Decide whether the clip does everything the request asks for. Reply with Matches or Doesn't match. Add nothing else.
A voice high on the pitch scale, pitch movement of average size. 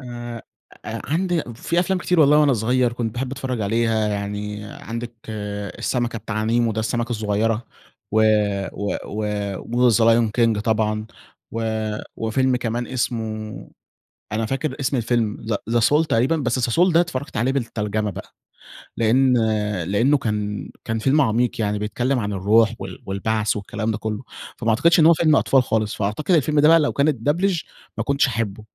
Doesn't match